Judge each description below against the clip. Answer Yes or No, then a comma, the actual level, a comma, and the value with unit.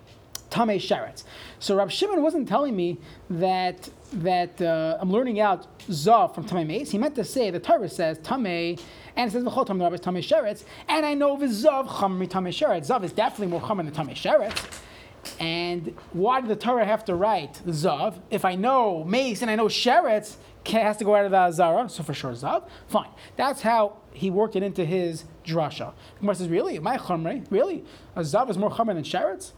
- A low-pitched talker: No, high, 200 Hz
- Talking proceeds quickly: Yes, fast, 210 wpm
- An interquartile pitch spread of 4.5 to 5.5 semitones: Yes, average, 5.2 semitones